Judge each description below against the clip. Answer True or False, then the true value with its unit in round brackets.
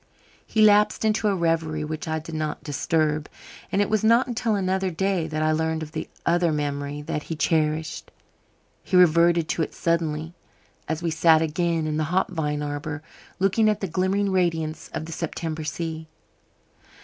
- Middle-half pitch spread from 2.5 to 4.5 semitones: True (3.0 semitones)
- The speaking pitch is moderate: True (160 Hz)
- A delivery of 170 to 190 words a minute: True (175 wpm)